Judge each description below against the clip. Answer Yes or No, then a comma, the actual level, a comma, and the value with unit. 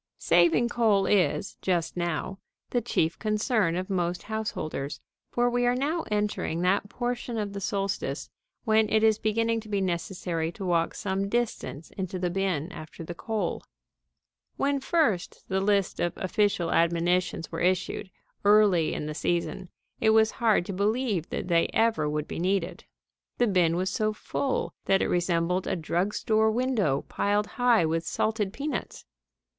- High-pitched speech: Yes, high, 195 Hz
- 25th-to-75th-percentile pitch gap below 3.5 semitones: No, average, 4.1 semitones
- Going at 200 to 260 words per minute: No, average, 160 wpm